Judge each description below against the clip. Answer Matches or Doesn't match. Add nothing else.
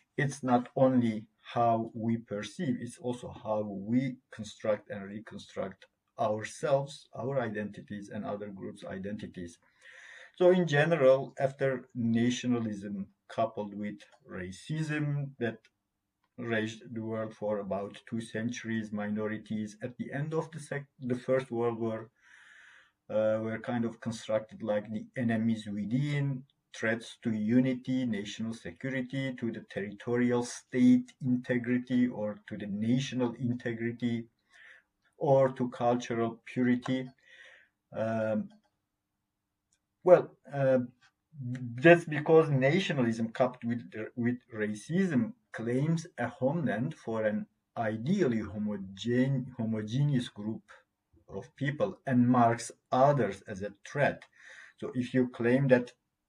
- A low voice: Matches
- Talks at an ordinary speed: Matches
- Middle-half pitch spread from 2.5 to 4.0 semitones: Matches